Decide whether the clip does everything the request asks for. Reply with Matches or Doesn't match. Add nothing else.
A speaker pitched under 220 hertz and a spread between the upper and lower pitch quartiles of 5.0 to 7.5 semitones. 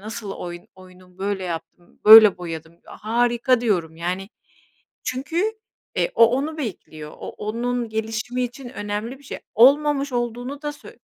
Doesn't match